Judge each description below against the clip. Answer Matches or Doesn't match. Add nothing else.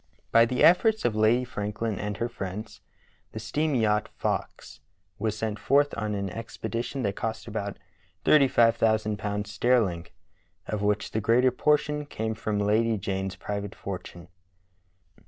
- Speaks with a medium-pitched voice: Doesn't match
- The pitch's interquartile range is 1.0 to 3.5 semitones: Matches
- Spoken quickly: Doesn't match